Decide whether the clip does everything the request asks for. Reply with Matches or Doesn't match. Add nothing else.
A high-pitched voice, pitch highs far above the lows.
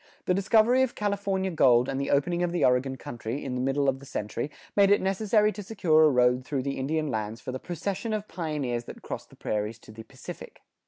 Doesn't match